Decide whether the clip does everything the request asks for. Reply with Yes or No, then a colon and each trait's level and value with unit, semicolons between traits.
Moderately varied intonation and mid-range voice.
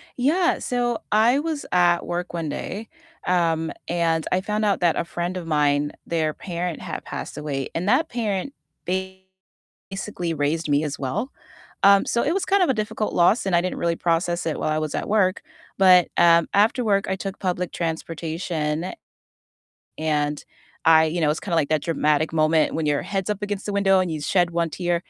Yes: average, 3.7 semitones; medium, 175 Hz